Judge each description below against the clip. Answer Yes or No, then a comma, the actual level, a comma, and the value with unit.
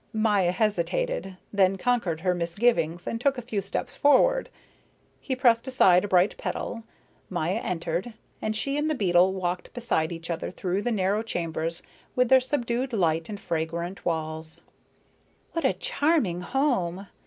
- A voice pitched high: Yes, high, 195 Hz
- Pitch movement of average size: No, wide, 5.9 semitones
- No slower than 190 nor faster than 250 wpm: No, average, 155 wpm